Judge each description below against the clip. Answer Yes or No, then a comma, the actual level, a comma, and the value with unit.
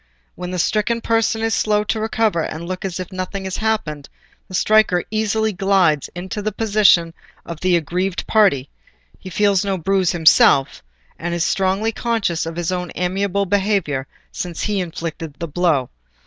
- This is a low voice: No, medium, 185 Hz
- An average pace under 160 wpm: No, average, 165 wpm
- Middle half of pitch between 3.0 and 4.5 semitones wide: Yes, average, 3.7 semitones